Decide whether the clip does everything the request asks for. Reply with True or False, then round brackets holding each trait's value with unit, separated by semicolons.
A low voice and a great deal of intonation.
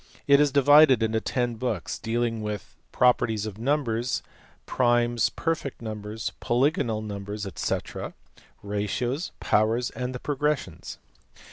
False (120 Hz; 3.3 semitones)